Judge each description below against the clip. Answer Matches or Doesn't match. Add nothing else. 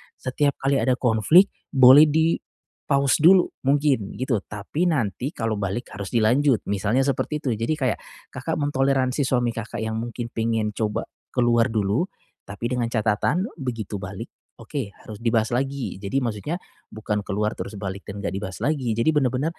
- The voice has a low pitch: Matches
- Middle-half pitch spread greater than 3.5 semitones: Matches